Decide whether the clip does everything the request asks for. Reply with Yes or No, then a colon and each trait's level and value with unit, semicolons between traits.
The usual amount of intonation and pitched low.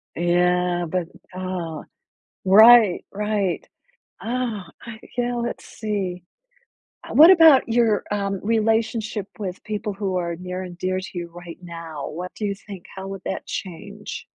No: average, 3.4 semitones; high, 195 Hz